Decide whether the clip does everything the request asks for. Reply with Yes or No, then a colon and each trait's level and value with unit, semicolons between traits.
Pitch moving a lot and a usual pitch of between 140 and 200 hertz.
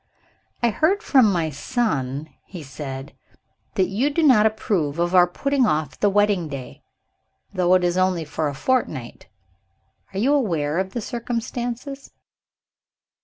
Yes: wide, 7.6 semitones; high, 190 Hz